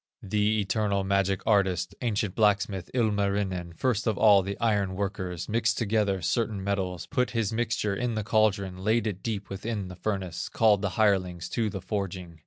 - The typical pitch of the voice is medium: No, low, 100 Hz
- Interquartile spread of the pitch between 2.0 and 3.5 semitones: Yes, narrow, 2.4 semitones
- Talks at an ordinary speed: Yes, average, 170 wpm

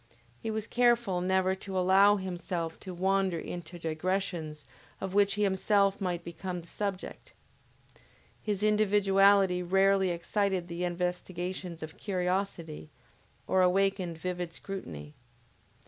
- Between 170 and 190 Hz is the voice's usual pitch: Yes, medium, 185 Hz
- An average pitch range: No, narrow, 2.1 semitones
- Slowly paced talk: Yes, slow, 115 wpm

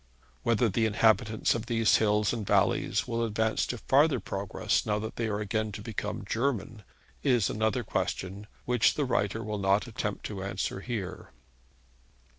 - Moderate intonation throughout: No, narrow, 2.1 semitones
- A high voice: No, low, 110 Hz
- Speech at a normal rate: Yes, average, 160 wpm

